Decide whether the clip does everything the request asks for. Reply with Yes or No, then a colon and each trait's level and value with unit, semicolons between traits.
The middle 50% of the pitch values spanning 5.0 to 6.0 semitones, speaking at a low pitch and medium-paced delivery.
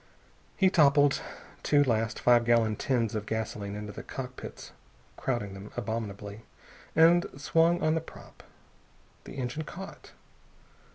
No: wide, 5.4 semitones; low, 120 Hz; slow, 125 wpm